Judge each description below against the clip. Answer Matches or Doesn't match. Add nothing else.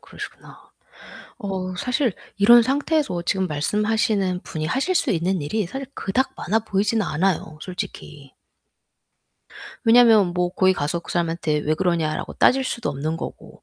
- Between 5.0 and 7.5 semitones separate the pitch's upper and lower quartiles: Matches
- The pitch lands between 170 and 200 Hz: Matches